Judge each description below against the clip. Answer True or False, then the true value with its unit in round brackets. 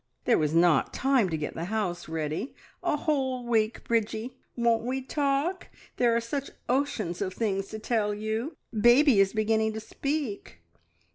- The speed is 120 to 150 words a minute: False (160 wpm)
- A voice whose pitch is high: True (225 Hz)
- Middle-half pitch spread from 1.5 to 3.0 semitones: False (4.7 semitones)